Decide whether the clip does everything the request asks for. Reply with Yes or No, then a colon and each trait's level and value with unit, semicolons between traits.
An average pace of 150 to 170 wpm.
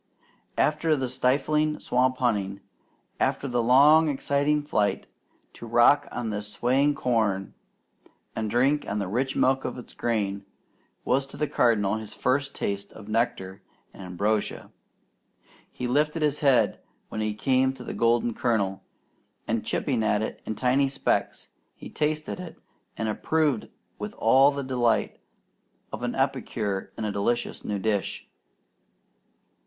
No: average, 140 wpm